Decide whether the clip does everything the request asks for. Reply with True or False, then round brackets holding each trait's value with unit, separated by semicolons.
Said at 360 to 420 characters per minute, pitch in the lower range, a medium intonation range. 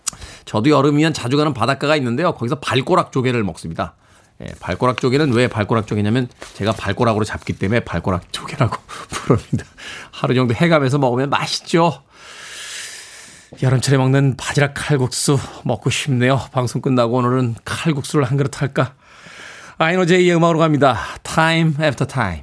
True (365 characters per minute; 130 Hz; 4.5 semitones)